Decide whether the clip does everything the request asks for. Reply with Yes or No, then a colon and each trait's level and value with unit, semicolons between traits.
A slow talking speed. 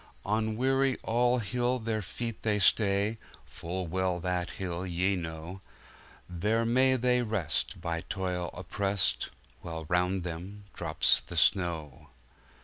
Yes: slow, 125 wpm